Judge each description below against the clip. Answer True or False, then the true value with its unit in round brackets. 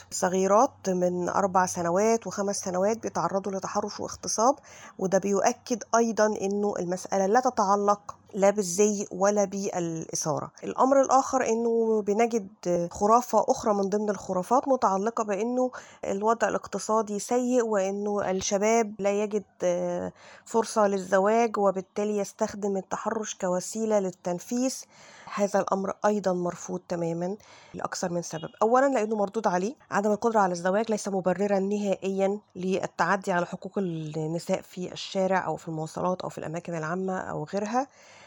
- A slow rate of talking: False (125 wpm)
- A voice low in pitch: False (200 Hz)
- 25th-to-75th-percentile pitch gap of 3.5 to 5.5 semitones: False (2.8 semitones)